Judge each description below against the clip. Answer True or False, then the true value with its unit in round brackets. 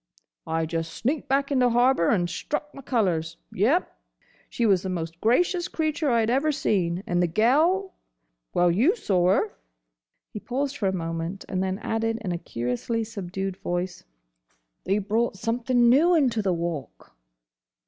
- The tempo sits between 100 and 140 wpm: False (160 wpm)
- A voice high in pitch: True (215 Hz)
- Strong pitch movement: True (6.8 semitones)